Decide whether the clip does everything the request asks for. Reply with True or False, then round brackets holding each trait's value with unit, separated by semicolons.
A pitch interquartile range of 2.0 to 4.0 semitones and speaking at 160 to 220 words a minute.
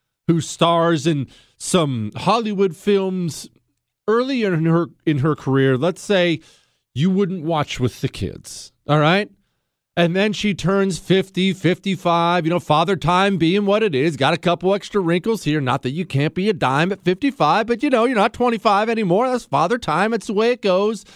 False (4.8 semitones; 185 wpm)